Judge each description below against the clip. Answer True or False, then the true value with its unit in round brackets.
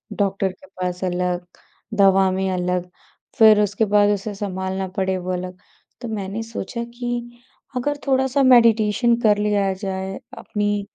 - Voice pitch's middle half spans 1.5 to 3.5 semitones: True (3.1 semitones)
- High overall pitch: True (200 Hz)